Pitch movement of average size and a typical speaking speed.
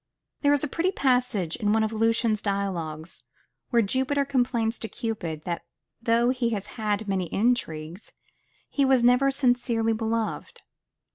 Yes: average, 3.8 semitones; average, 150 wpm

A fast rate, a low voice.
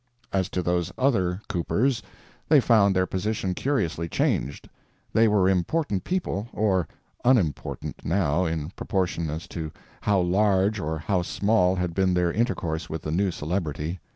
No: average, 145 wpm; very low, 95 Hz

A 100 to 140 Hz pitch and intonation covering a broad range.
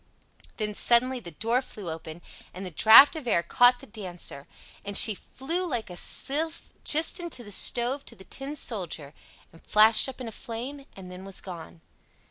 No: high, 225 Hz; wide, 6.2 semitones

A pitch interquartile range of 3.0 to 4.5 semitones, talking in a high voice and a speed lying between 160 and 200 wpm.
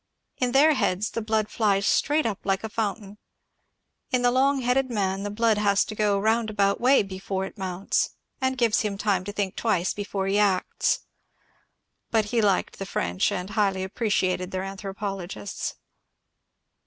No: narrow, 2.6 semitones; high, 205 Hz; average, 165 wpm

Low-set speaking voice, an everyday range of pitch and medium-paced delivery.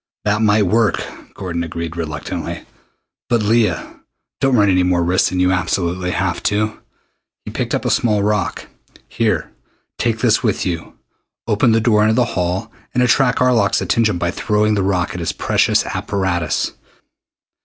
Yes: low, 100 Hz; average, 3.6 semitones; average, 160 wpm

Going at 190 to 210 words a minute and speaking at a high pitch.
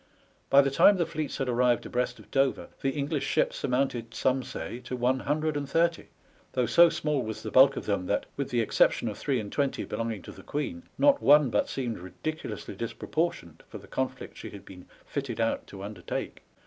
No: fast, 205 wpm; low, 130 Hz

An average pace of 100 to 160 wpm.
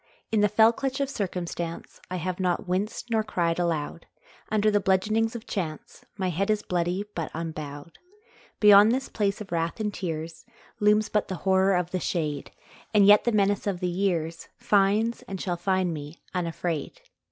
No: average, 175 wpm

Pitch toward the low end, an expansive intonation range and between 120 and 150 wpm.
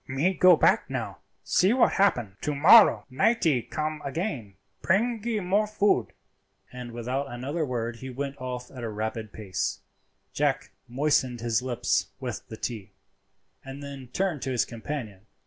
Yes: low, 130 Hz; wide, 5.7 semitones; average, 145 wpm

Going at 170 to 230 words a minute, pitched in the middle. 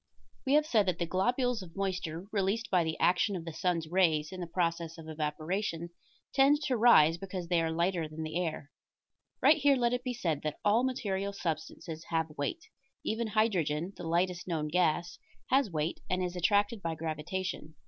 Yes: average, 185 wpm; medium, 180 Hz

